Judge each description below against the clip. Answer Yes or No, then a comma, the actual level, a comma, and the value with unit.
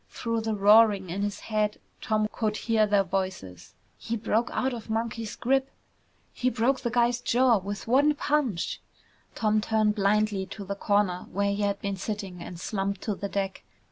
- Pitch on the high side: Yes, high, 210 Hz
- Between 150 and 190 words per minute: Yes, average, 175 wpm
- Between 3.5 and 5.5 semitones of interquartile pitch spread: No, narrow, 2.5 semitones